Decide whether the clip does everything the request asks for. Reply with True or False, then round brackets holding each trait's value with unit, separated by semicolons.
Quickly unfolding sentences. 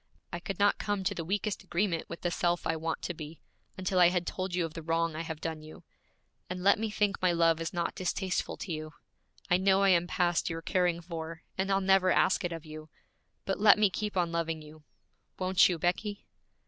True (225 wpm)